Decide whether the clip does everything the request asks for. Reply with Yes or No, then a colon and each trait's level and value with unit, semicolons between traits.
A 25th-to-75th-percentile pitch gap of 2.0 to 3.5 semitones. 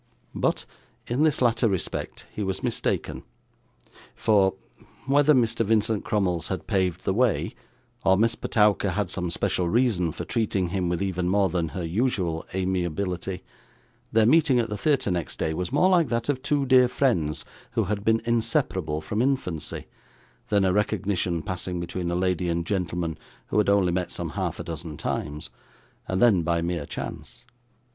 No: average, 4.6 semitones